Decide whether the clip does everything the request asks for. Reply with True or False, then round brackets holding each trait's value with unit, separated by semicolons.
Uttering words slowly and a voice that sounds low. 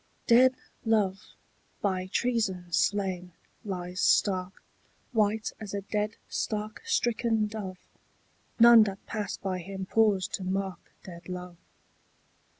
False (115 wpm; 200 Hz)